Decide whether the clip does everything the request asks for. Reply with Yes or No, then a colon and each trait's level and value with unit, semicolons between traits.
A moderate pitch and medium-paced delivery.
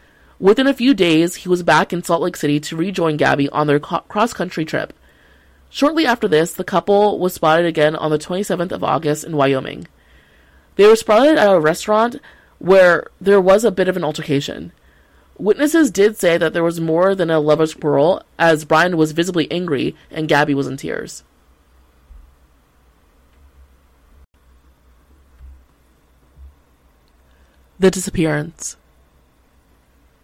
Yes: medium, 150 Hz; average, 145 wpm